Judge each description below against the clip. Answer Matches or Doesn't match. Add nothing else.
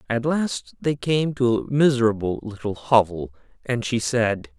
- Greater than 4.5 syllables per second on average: Doesn't match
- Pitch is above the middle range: Doesn't match